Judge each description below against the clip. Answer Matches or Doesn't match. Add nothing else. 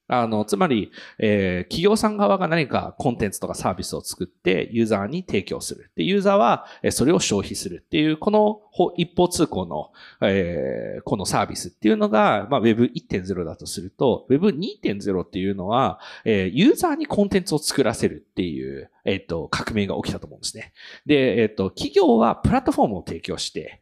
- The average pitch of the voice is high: Doesn't match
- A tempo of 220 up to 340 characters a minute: Doesn't match